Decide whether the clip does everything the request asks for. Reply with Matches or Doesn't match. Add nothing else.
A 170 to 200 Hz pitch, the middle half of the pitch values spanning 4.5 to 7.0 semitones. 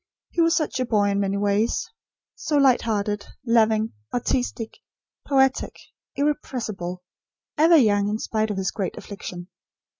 Doesn't match